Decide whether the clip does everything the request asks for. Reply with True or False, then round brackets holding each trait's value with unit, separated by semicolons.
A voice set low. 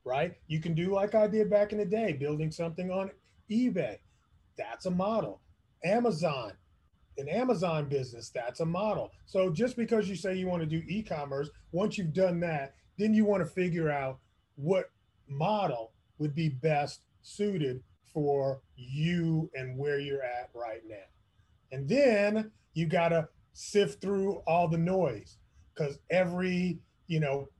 False (165 Hz)